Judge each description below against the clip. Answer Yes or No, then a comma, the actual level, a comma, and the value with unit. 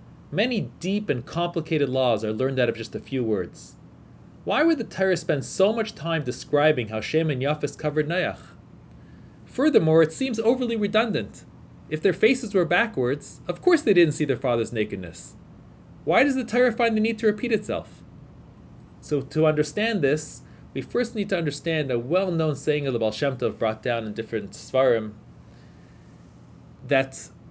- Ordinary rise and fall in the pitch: No, wide, 9.0 semitones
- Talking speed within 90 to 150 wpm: No, average, 175 wpm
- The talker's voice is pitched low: No, medium, 155 Hz